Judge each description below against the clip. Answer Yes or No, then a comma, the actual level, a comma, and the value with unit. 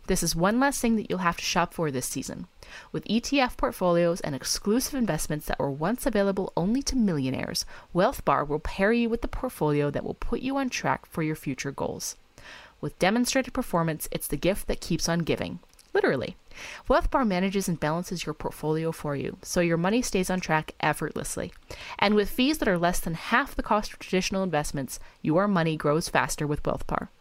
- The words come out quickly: No, average, 195 wpm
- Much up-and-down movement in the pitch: Yes, wide, 6.9 semitones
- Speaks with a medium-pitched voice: Yes, medium, 180 Hz